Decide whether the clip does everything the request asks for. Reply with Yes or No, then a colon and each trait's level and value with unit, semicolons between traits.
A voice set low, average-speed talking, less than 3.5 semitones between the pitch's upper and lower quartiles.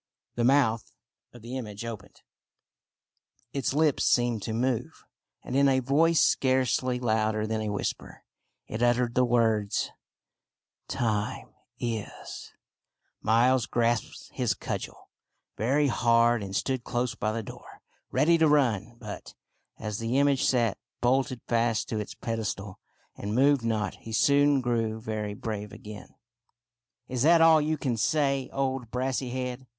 Yes: low, 120 Hz; average, 145 wpm; average, 3.1 semitones